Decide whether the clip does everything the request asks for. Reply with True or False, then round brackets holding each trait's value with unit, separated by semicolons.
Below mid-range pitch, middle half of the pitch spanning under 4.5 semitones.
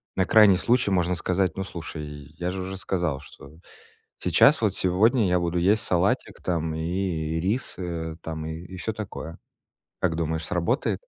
True (90 Hz; 2.9 semitones)